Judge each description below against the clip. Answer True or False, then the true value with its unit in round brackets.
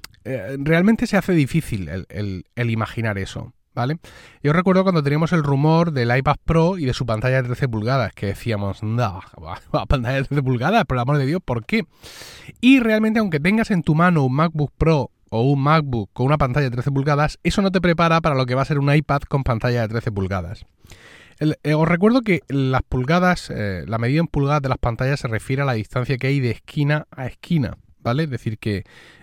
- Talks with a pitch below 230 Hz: True (140 Hz)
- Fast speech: True (220 wpm)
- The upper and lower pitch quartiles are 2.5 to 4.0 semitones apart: False (5.3 semitones)